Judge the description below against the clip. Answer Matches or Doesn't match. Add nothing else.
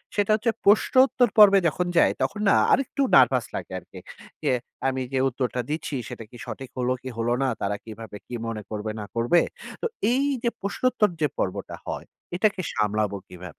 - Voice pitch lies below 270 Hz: Matches